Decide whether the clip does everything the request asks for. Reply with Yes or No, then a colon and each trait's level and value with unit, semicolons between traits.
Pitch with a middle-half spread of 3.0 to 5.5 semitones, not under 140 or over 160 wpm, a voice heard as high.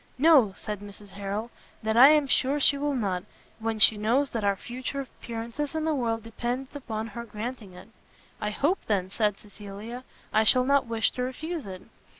No: average, 4.3 semitones; average, 185 wpm; high, 230 Hz